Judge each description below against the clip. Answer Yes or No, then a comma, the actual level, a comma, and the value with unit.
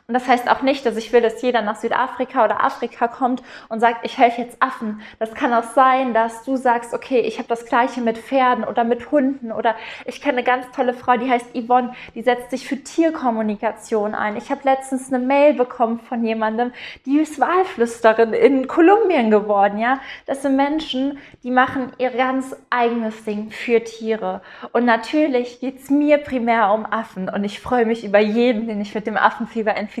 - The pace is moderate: No, fast, 200 wpm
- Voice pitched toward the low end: No, high, 240 Hz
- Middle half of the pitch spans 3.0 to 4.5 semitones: No, narrow, 2.5 semitones